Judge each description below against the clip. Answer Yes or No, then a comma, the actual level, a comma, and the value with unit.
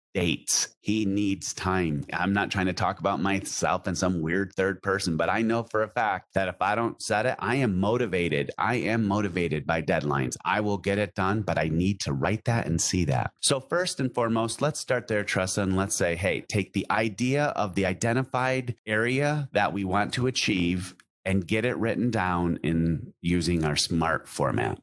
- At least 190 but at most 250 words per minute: Yes, fast, 205 wpm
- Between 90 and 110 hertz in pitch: Yes, low, 100 Hz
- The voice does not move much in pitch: No, average, 4.0 semitones